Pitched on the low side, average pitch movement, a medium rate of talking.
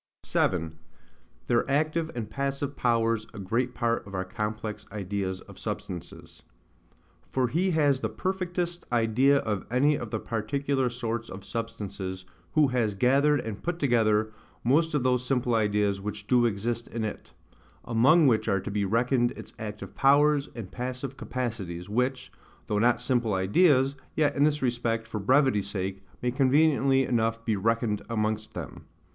Yes: low, 120 Hz; average, 4.3 semitones; average, 155 wpm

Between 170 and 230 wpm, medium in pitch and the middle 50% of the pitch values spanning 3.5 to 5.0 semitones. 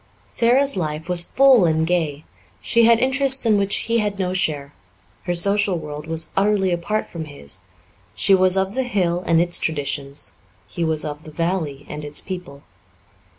Yes: average, 175 wpm; medium, 175 Hz; average, 4.7 semitones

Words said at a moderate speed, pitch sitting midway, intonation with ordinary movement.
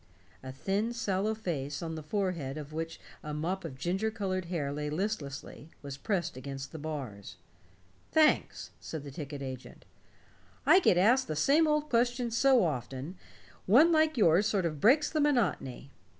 No: average, 165 wpm; medium, 175 Hz; wide, 7.6 semitones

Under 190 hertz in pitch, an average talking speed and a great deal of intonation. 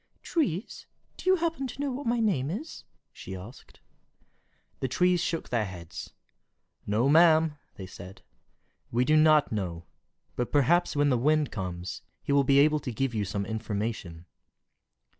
Yes: medium, 140 Hz; average, 160 wpm; wide, 8.4 semitones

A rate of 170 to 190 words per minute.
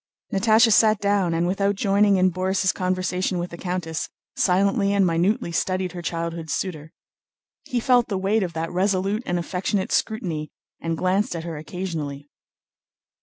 No: average, 155 wpm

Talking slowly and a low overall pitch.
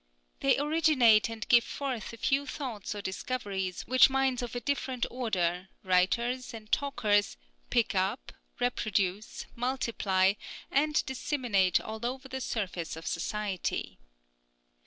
No: slow, 125 wpm; high, 230 Hz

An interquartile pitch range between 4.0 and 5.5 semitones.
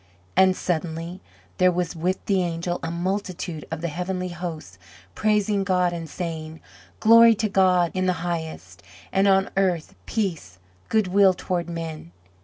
No: narrow, 2.5 semitones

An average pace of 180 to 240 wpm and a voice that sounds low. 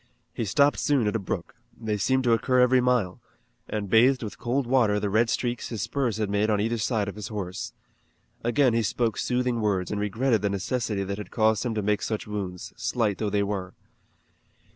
Yes: fast, 205 wpm; low, 110 Hz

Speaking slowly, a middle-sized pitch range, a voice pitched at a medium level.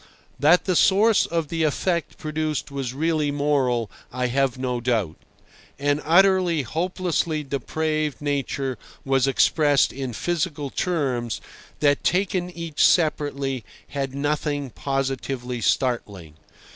Yes: slow, 115 wpm; average, 3.4 semitones; medium, 145 Hz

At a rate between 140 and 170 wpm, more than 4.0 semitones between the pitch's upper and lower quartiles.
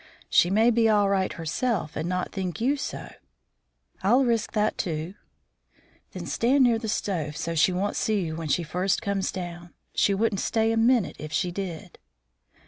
No: average, 180 wpm; average, 4.4 semitones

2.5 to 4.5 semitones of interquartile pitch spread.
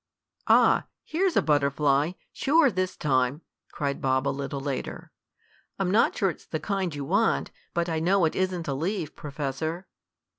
No: average, 5.0 semitones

